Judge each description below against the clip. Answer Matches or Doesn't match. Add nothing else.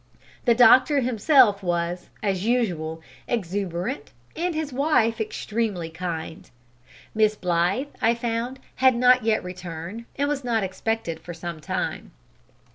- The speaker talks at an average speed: Doesn't match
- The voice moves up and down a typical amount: Doesn't match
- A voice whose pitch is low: Doesn't match